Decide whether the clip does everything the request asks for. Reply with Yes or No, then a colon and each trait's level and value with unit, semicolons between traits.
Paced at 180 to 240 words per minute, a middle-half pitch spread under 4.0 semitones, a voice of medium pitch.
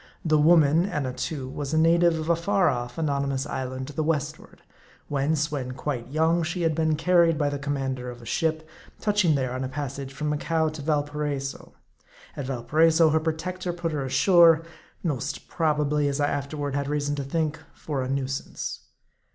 Yes: average, 185 wpm; average, 2.7 semitones; medium, 150 Hz